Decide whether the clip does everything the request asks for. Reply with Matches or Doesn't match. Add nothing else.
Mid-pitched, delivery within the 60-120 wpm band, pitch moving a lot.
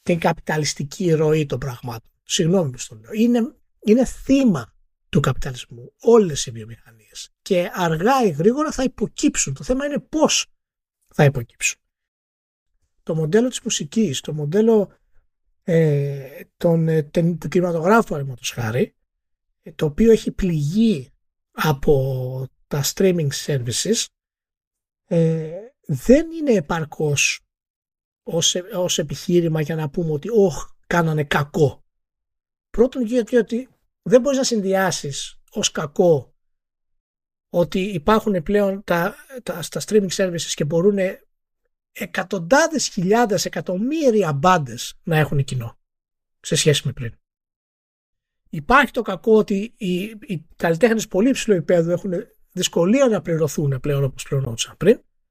Matches